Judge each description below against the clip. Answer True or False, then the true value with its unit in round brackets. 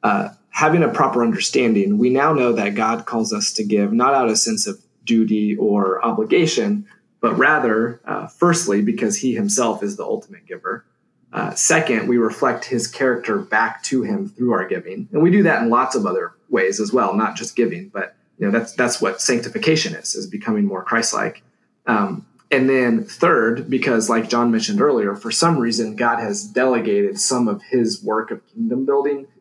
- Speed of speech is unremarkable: True (190 wpm)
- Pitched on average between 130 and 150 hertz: True (135 Hz)